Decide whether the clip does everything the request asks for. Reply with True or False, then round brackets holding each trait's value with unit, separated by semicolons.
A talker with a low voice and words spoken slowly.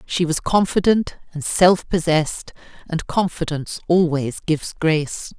False (165 Hz; 125 wpm)